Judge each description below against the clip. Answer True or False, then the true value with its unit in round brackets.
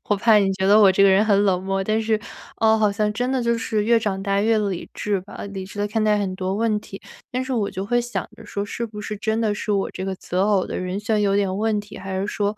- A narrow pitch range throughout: True (2.0 semitones)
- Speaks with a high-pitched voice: True (205 Hz)